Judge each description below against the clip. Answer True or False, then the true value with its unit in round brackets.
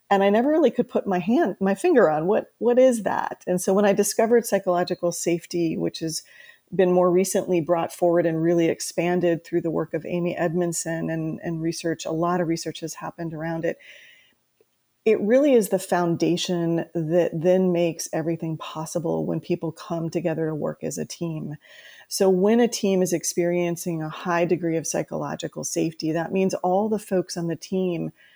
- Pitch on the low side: False (175 Hz)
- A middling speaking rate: True (185 wpm)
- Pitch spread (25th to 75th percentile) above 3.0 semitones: False (2.5 semitones)